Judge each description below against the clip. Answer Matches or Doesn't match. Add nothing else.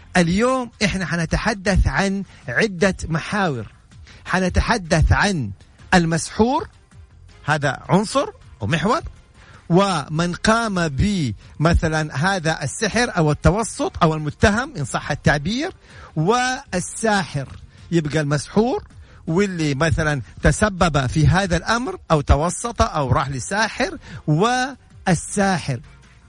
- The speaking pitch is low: Doesn't match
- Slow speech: Matches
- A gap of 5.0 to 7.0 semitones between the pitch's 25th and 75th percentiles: Matches